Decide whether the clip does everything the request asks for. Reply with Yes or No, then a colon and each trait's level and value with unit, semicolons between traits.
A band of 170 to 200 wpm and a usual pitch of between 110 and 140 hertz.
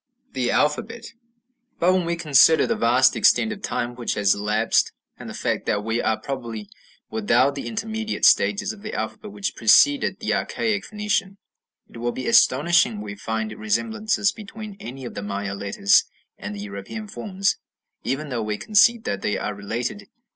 Yes: average, 175 wpm; low, 135 Hz